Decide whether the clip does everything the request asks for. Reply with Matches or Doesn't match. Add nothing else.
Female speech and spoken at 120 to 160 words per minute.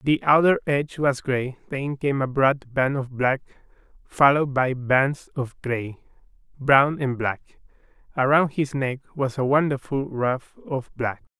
Doesn't match